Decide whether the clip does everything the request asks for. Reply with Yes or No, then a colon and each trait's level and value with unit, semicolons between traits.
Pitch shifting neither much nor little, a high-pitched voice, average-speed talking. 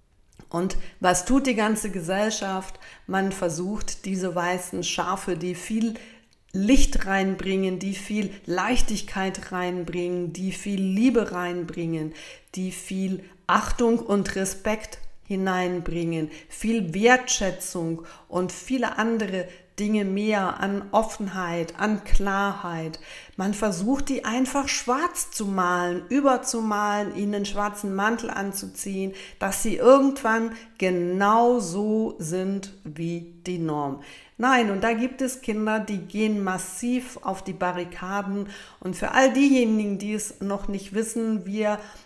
No: average, 3.2 semitones; high, 195 Hz; slow, 120 wpm